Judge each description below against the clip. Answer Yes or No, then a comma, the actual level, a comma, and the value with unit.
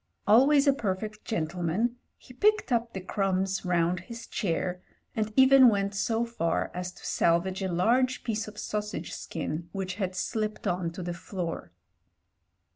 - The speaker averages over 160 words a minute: No, average, 155 wpm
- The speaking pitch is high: Yes, high, 195 Hz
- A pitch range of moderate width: Yes, average, 4.4 semitones